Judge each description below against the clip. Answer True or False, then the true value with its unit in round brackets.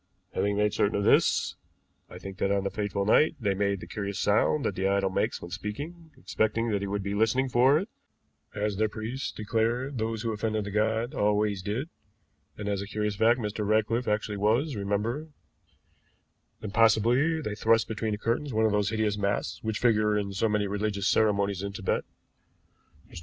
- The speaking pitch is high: False (105 Hz)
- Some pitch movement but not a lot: False (2.1 semitones)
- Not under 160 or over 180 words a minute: False (190 wpm)